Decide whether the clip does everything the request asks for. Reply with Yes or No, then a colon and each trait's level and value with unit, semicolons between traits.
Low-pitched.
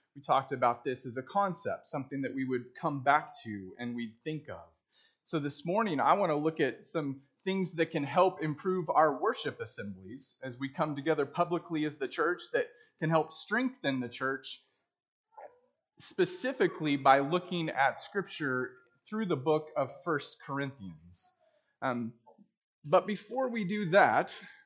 No: medium, 155 Hz